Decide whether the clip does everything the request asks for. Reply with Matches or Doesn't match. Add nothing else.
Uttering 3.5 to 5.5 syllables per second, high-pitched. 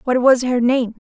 Matches